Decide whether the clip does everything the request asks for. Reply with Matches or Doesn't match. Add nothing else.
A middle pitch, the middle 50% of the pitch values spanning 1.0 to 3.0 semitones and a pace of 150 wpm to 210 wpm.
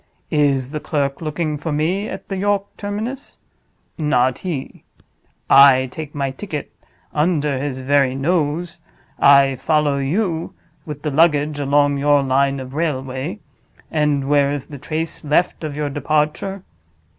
Doesn't match